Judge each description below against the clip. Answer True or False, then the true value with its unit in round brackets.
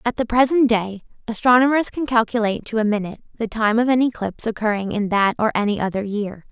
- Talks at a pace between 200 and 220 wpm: True (205 wpm)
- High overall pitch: True (225 Hz)